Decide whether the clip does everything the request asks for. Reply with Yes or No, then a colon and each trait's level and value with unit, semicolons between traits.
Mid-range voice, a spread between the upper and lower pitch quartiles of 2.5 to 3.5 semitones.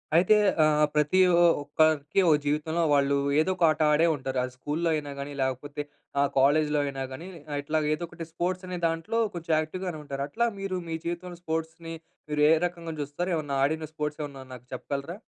Yes: medium, 155 Hz; average, 2.9 semitones